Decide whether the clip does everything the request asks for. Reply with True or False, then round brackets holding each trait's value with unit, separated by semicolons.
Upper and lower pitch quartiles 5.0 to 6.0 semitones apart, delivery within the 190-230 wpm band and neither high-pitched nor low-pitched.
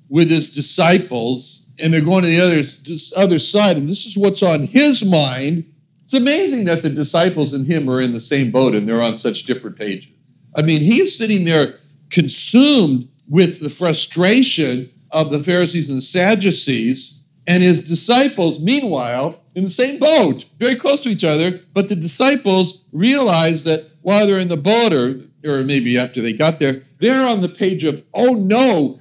False (5.4 semitones; 180 wpm; 170 Hz)